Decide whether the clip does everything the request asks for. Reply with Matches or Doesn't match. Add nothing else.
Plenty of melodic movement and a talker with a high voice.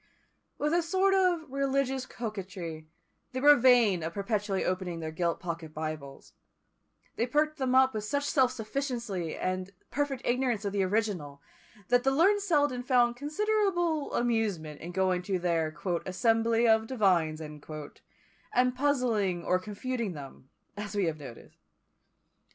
Matches